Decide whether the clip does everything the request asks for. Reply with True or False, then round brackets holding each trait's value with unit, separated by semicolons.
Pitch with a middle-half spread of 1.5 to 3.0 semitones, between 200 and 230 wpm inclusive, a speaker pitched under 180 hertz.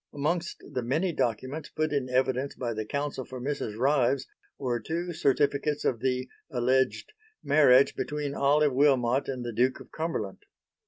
False (2.7 semitones; 155 wpm; 135 Hz)